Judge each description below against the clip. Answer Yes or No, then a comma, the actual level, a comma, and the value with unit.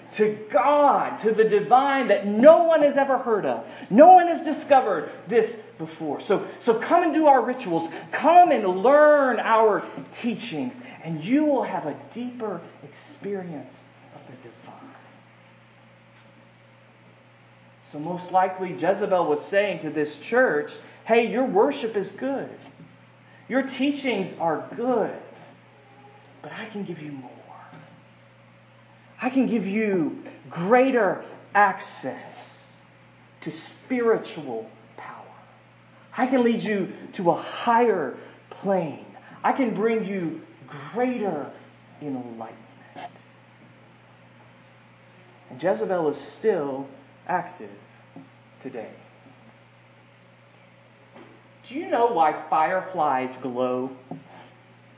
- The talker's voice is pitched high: Yes, high, 200 Hz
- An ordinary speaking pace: No, slow, 110 wpm